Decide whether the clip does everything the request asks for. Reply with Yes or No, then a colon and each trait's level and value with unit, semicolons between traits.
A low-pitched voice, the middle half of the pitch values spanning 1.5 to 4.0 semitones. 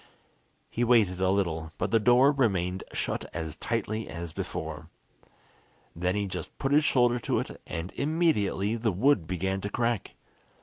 No: low, 100 Hz; average, 5.0 semitones